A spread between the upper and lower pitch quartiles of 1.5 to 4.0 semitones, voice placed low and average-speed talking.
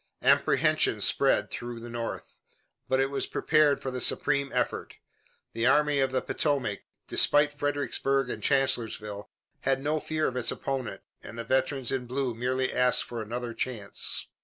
Yes: average, 2.7 semitones; low, 130 Hz; average, 160 wpm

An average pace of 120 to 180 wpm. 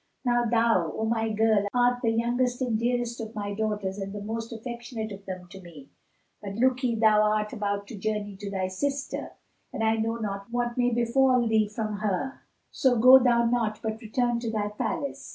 No: average, 195 wpm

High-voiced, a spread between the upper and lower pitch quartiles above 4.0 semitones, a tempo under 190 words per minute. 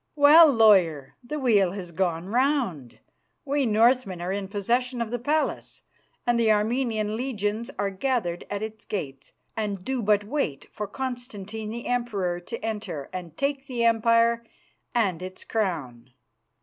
Yes: high, 220 Hz; average, 4.5 semitones; average, 150 wpm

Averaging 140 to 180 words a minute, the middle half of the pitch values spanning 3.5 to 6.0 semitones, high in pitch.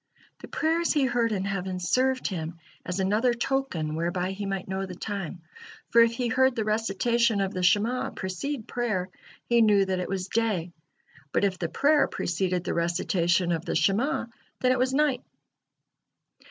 Yes: average, 175 wpm; average, 4.9 semitones; high, 200 Hz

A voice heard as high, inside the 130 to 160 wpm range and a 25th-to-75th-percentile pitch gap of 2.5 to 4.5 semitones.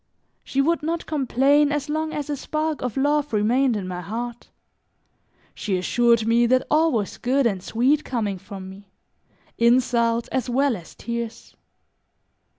Yes: high, 245 Hz; average, 155 wpm; average, 4.2 semitones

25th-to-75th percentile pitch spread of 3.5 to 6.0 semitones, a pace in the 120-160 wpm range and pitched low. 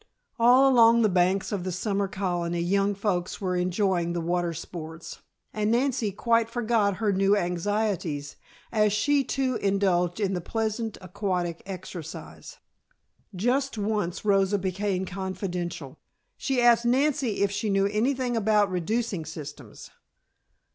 No: average, 3.9 semitones; slow, 135 wpm; high, 200 Hz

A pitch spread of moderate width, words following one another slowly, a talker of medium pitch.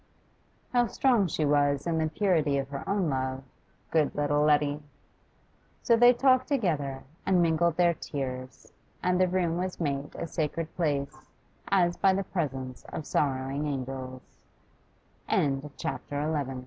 Yes: average, 4.5 semitones; slow, 125 wpm; medium, 160 Hz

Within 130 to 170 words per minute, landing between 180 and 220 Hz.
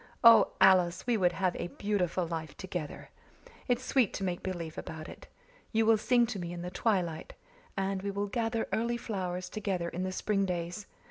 No: average, 190 wpm; high, 190 Hz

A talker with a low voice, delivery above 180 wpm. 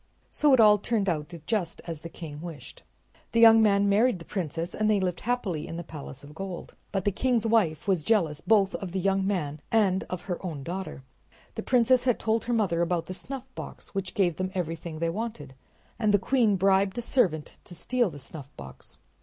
No: high, 190 Hz; fast, 205 wpm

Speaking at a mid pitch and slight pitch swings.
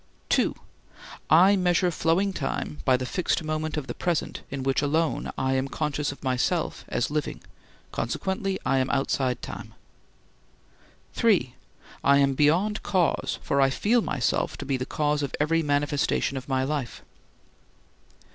No: medium, 145 Hz; average, 3.5 semitones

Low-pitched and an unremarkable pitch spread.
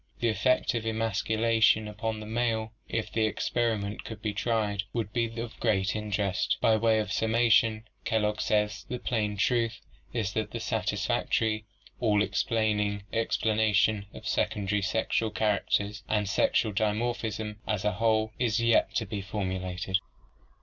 No: low, 110 Hz; narrow, 1.5 semitones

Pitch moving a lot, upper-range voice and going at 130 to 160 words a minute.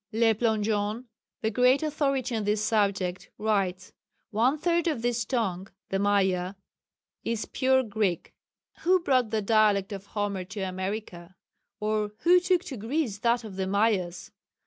No: average, 3.6 semitones; high, 215 Hz; average, 145 wpm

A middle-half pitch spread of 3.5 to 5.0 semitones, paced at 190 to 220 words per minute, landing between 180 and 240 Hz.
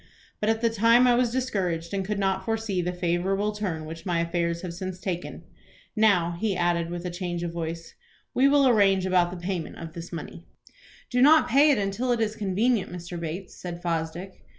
Yes: average, 4.1 semitones; average, 200 wpm; medium, 185 Hz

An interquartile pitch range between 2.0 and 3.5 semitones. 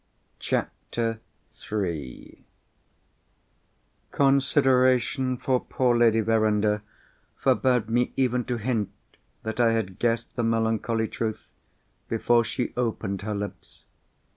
Yes: narrow, 2.4 semitones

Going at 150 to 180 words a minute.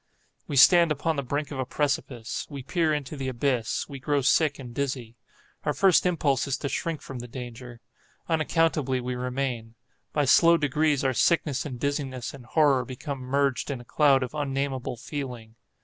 Yes: average, 175 wpm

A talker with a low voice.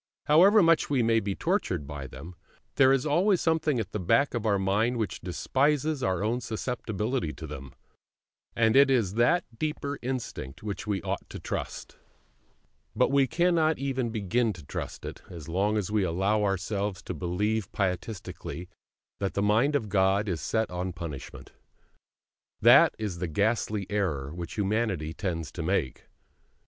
Yes: low, 105 Hz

